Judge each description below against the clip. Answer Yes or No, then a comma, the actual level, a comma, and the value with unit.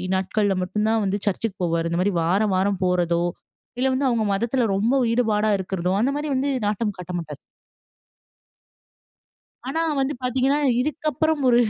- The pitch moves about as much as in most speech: No, wide, 5.7 semitones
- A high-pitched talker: Yes, high, 215 Hz